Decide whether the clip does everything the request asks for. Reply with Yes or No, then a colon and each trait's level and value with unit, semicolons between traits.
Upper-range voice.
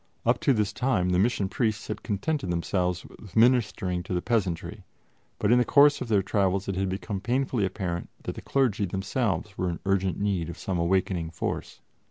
No: low, 100 Hz